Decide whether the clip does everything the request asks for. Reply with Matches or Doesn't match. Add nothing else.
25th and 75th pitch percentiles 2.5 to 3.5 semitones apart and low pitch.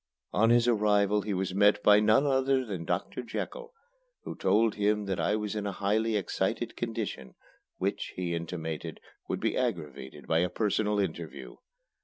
Matches